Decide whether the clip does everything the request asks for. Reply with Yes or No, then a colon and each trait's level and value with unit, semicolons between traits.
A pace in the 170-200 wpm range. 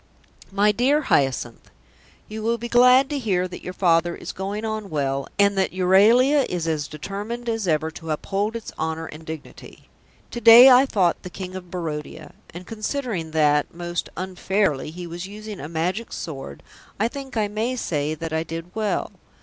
Yes: average, 180 wpm